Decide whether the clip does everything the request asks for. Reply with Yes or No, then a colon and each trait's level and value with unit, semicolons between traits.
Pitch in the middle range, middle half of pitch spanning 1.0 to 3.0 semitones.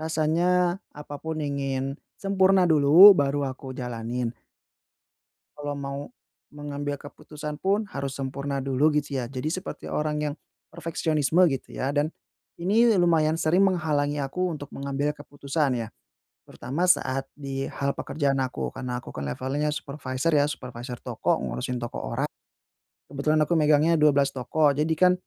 Yes: medium, 145 Hz; narrow, 2.6 semitones